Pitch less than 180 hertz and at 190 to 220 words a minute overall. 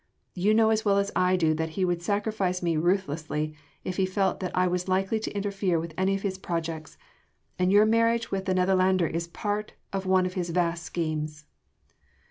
No: medium, 185 Hz; average, 200 wpm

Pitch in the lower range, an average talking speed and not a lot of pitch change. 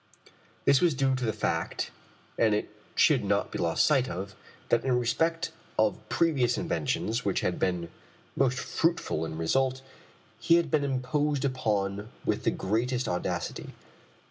No: low, 125 Hz; average, 150 wpm; average, 5.3 semitones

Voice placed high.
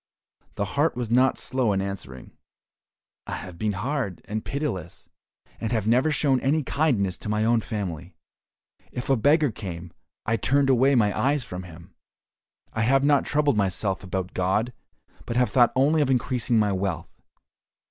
No: low, 115 Hz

